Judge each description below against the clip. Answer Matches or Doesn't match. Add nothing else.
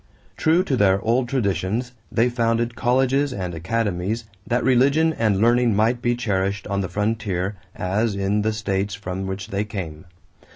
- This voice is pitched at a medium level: Doesn't match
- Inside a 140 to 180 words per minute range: Matches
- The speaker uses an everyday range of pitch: Matches